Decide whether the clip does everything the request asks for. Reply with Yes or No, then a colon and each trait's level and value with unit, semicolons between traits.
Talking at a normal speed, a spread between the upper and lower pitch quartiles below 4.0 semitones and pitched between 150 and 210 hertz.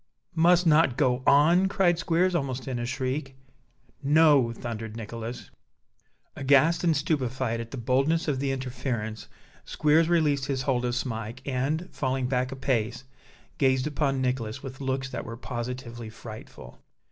No: average, 145 wpm; average, 3.5 semitones; low, 130 Hz